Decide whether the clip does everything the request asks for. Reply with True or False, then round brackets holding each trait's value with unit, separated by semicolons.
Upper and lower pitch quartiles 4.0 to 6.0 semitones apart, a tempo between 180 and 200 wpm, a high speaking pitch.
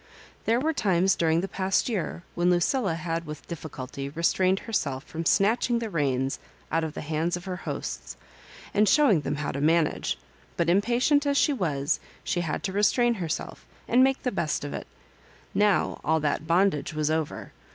False (5.1 semitones; 185 wpm; 170 Hz)